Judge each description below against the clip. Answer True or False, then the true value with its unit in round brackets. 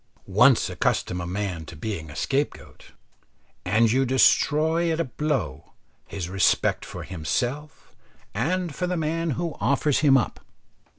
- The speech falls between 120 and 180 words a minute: True (140 wpm)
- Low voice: True (130 Hz)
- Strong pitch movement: True (8.2 semitones)